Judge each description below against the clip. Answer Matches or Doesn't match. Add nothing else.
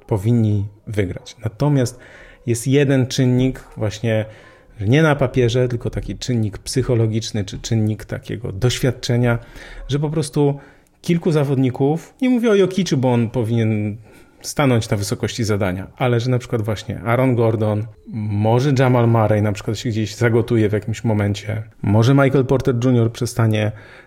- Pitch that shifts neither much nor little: Matches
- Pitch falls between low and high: Doesn't match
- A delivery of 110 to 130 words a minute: Doesn't match